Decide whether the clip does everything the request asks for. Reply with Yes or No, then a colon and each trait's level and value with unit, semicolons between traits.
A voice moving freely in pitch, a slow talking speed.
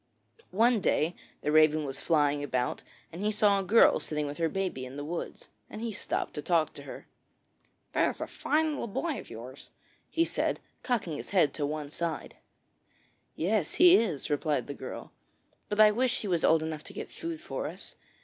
No: wide, 6.4 semitones; average, 195 wpm